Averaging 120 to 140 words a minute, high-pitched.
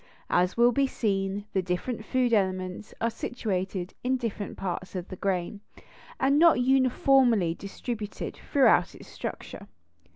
Yes: slow, 135 wpm; high, 210 Hz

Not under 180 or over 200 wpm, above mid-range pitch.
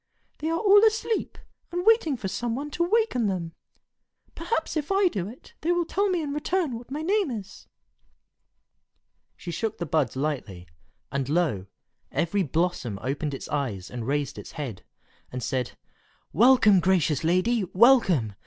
No: average, 160 wpm; high, 200 Hz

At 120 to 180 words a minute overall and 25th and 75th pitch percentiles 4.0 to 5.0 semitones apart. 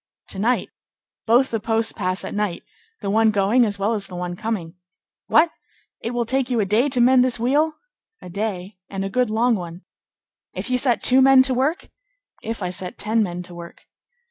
No: fast, 205 wpm; average, 4.4 semitones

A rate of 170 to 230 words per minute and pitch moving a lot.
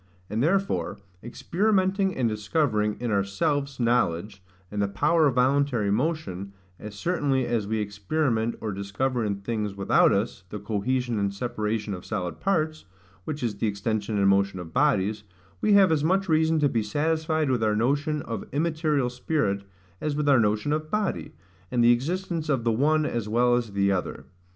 Yes: average, 175 wpm; wide, 6.7 semitones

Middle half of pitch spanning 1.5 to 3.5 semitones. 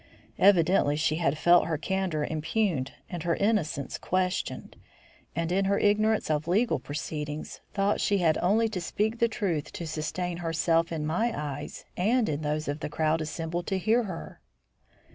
No: average, 4.3 semitones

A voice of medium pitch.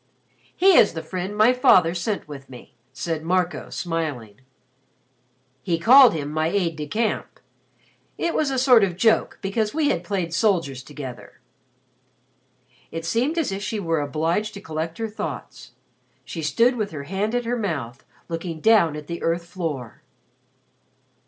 Yes: medium, 175 Hz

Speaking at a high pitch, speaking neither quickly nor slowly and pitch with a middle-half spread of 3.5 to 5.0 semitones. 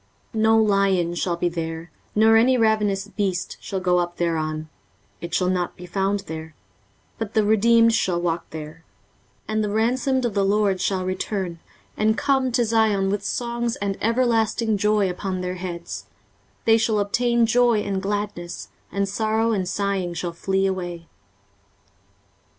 Yes: high, 200 Hz; average, 160 wpm; average, 3.8 semitones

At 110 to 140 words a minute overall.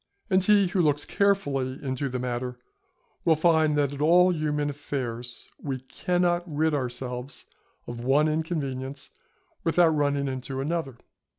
Yes: slow, 135 wpm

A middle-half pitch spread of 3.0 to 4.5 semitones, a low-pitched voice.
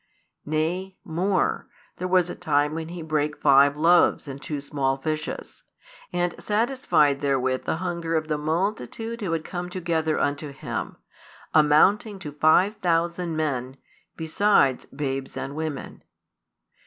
No: average, 3.5 semitones; medium, 160 Hz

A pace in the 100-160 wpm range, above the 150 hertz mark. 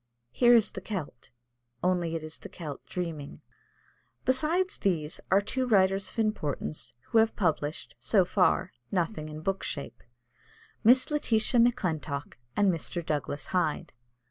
Yes: average, 140 wpm; medium, 185 Hz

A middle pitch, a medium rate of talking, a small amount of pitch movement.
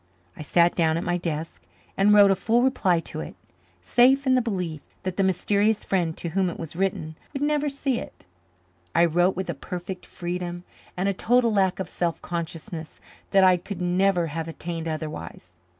No: medium, 180 Hz; average, 190 wpm; average, 3.1 semitones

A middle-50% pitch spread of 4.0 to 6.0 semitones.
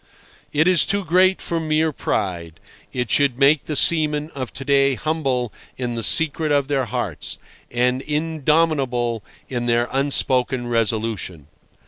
Yes: average, 4.3 semitones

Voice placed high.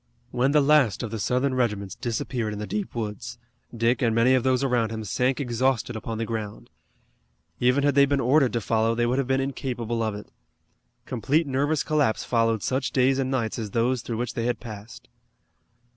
No: low, 120 Hz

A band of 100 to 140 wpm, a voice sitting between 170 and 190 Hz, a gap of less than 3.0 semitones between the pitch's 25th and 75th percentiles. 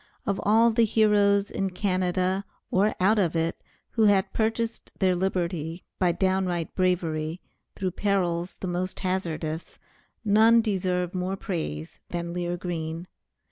Yes: slow, 135 wpm; medium, 185 Hz; narrow, 2.6 semitones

